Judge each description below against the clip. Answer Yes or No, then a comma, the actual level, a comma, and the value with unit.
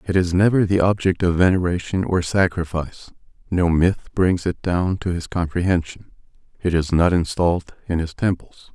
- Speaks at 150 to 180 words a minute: Yes, average, 165 wpm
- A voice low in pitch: Yes, very low, 90 Hz